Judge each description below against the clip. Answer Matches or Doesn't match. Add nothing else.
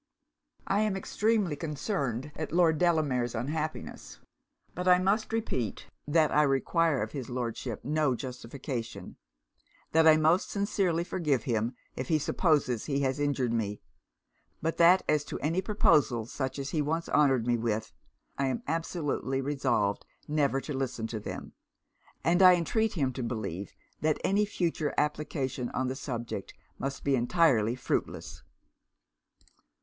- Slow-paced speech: Doesn't match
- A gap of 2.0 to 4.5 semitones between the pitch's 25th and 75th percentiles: Doesn't match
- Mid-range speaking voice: Matches